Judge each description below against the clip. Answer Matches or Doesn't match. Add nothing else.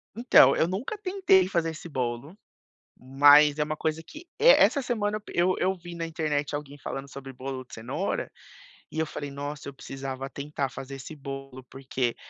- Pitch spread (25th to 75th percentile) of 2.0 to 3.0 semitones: Doesn't match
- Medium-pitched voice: Matches